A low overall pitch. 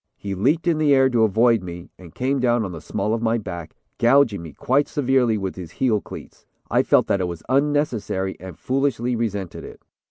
Yes: low, 115 Hz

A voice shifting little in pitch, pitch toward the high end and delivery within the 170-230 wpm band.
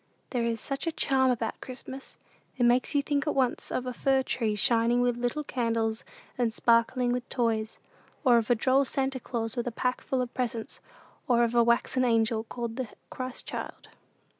Yes: narrow, 2.0 semitones; high, 245 Hz; average, 190 wpm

